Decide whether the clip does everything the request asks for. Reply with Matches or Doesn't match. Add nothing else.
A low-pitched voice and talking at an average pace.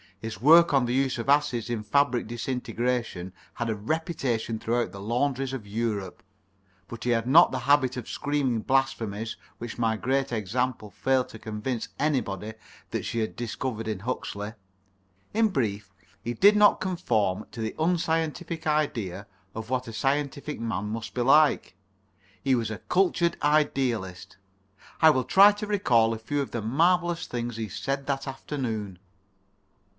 Matches